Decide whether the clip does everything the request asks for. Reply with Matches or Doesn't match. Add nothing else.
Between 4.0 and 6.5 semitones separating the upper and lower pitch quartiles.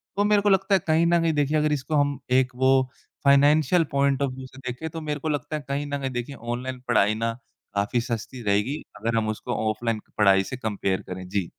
Matches